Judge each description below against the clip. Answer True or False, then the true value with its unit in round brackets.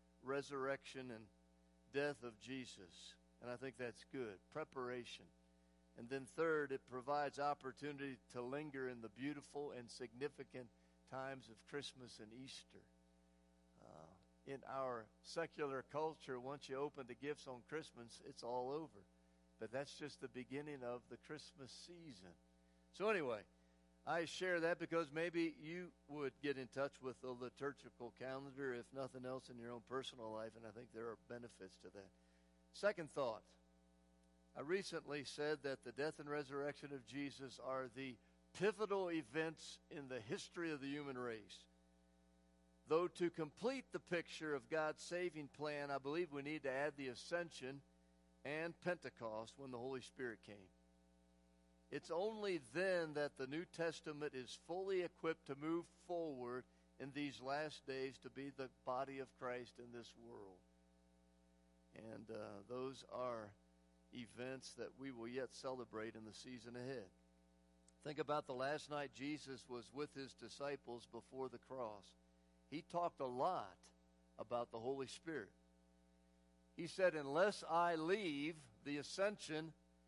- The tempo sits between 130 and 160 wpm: True (150 wpm)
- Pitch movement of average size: False (6.3 semitones)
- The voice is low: True (130 Hz)